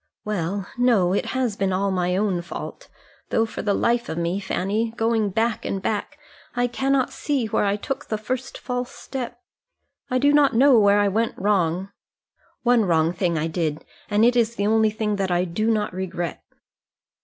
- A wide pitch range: No, average, 4.1 semitones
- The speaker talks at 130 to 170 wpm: No, average, 190 wpm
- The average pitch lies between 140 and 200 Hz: No, high, 210 Hz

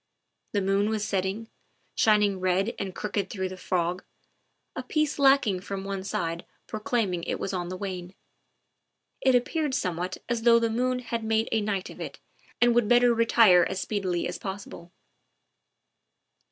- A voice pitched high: Yes, high, 205 Hz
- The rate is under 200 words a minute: Yes, average, 165 wpm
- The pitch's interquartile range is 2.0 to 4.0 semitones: Yes, average, 3.7 semitones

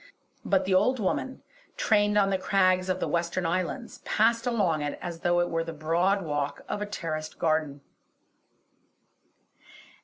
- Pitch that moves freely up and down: No, average, 3.7 semitones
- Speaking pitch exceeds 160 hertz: Yes, medium, 185 Hz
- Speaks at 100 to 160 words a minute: Yes, average, 155 wpm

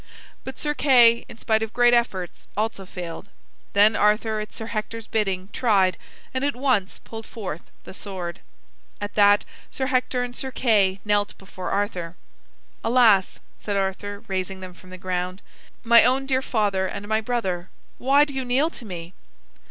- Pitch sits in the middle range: No, high, 210 Hz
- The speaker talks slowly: No, average, 165 wpm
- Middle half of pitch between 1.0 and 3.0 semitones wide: No, average, 4.3 semitones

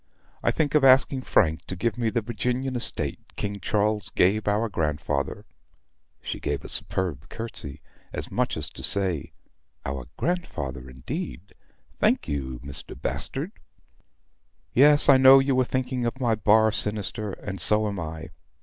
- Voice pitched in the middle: No, low, 105 Hz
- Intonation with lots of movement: Yes, wide, 7.7 semitones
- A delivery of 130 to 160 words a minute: Yes, average, 150 wpm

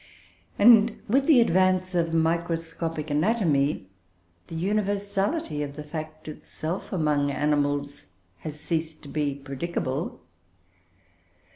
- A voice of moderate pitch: Yes, medium, 160 Hz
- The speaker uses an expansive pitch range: No, average, 4.0 semitones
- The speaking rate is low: Yes, slow, 105 wpm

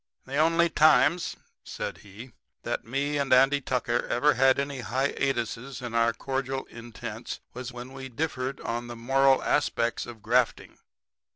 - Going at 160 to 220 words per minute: No, average, 150 wpm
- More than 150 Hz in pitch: No, low, 130 Hz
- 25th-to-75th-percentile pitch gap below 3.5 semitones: Yes, narrow, 2.4 semitones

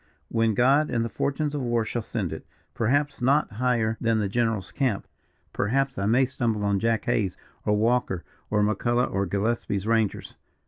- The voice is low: Yes, low, 115 Hz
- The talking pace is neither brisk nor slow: Yes, average, 175 wpm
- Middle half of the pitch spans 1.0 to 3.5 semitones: Yes, average, 3.1 semitones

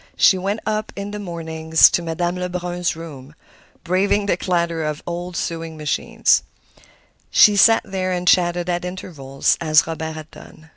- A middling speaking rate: Yes, average, 160 wpm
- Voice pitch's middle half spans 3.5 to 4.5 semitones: No, narrow, 2.4 semitones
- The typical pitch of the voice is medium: Yes, medium, 175 Hz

